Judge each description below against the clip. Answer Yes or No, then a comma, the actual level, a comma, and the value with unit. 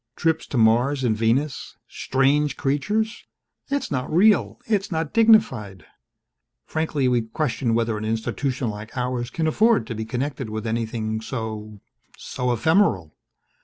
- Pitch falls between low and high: No, low, 125 Hz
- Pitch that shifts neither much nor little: No, wide, 5.9 semitones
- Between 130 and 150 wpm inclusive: Yes, slow, 135 wpm